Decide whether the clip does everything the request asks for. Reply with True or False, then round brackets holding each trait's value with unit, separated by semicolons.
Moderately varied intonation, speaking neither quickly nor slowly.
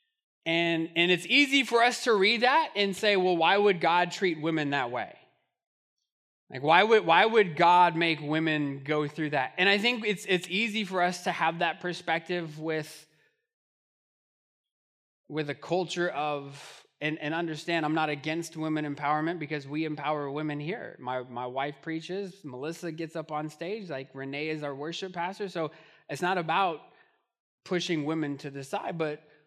True (3.2 semitones; 175 wpm)